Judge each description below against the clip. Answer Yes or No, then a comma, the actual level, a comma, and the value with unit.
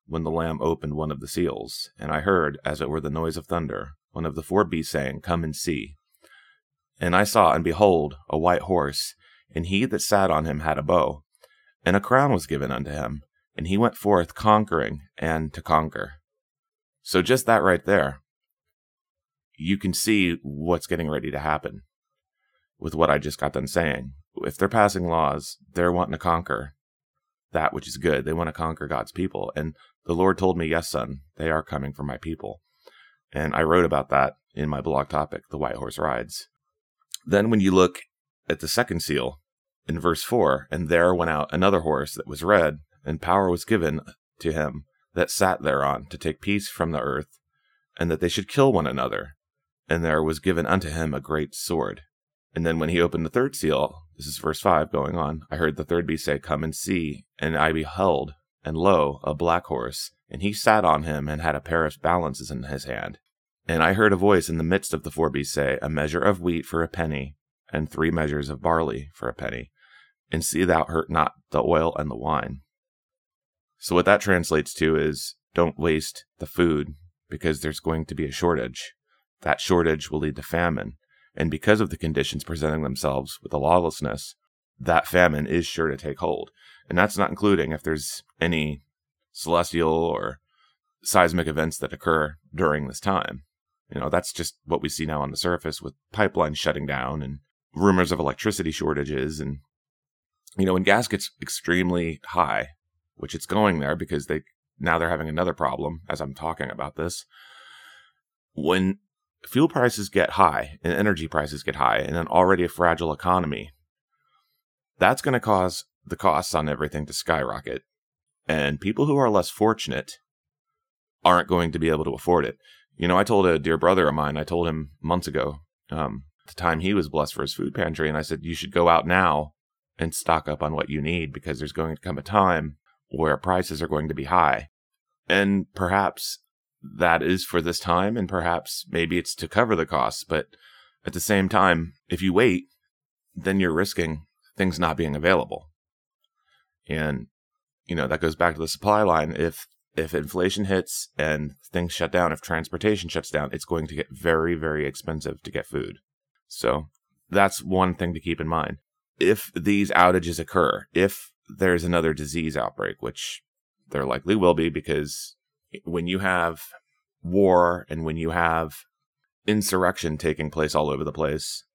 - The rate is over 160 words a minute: Yes, average, 190 wpm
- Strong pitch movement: No, average, 3.4 semitones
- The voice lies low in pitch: Yes, very low, 80 Hz